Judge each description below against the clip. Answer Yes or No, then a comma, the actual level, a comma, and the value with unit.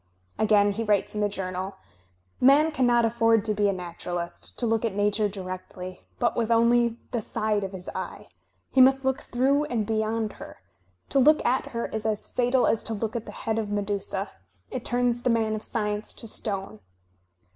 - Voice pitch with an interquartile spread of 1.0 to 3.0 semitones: Yes, average, 2.7 semitones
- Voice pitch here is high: Yes, high, 220 Hz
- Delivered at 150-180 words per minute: No, average, 190 wpm